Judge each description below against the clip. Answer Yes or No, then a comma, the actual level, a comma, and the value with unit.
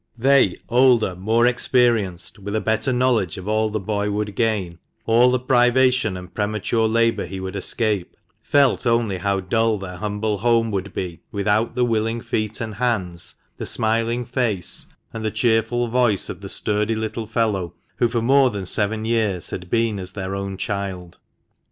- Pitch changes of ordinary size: Yes, average, 3.0 semitones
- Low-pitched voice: Yes, low, 110 Hz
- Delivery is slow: No, average, 175 wpm